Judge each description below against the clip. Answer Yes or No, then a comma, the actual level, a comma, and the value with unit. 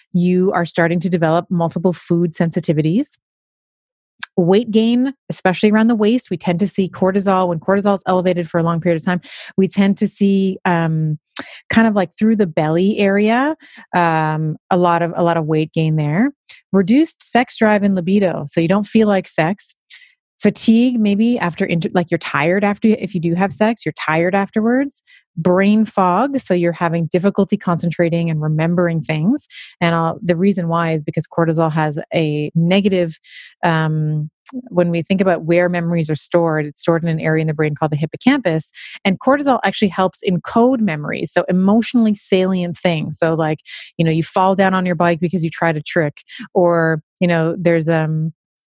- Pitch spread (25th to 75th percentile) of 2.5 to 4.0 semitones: Yes, average, 3.4 semitones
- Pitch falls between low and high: Yes, medium, 180 Hz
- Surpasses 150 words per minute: Yes, average, 180 wpm